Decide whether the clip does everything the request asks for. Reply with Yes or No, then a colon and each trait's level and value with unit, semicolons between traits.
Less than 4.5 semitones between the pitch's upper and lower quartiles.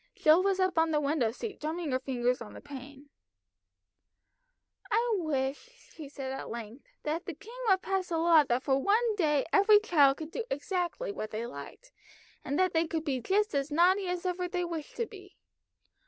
No: wide, 5.6 semitones